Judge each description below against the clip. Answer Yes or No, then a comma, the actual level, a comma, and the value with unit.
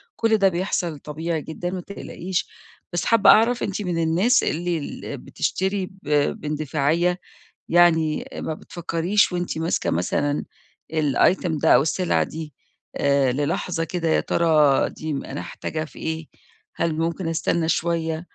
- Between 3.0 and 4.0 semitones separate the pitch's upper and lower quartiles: No, narrow, 2.5 semitones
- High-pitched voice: No, medium, 165 Hz